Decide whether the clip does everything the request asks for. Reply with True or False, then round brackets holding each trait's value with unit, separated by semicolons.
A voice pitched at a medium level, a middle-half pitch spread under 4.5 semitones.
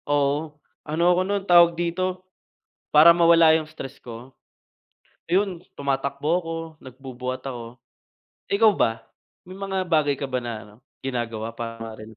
False (150 Hz; 5.4 semitones)